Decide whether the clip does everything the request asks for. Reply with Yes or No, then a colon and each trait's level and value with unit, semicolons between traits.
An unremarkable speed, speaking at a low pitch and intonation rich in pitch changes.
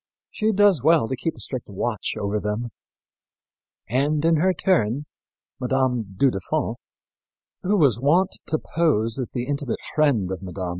Yes: average, 155 wpm; low, 130 Hz; wide, 6.2 semitones